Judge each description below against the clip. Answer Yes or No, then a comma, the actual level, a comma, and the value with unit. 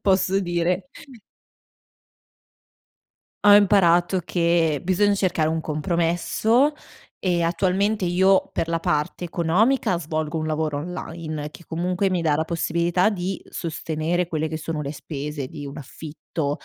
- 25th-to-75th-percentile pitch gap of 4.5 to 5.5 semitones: No, average, 2.8 semitones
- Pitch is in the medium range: Yes, medium, 170 Hz